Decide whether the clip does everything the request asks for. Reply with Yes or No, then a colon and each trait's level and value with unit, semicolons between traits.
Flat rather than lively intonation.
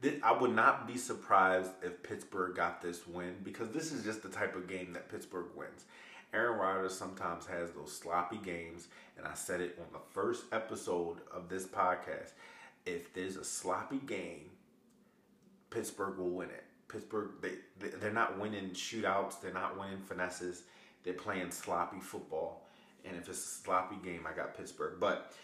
Yes: narrow, 1.7 semitones